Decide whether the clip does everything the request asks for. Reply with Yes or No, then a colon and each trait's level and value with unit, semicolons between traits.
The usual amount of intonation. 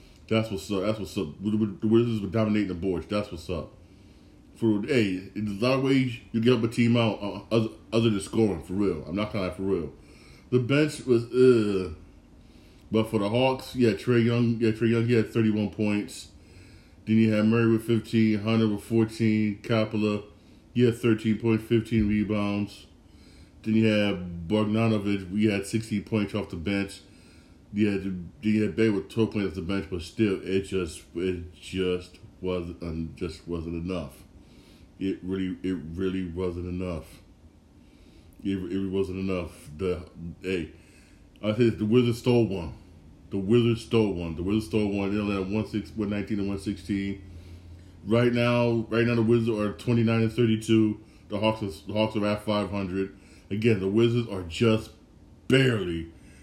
Yes: average, 3.4 semitones